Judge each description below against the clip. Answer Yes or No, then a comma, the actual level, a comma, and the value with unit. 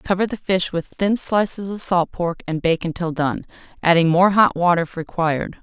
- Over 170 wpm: Yes, fast, 205 wpm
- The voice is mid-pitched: Yes, medium, 180 Hz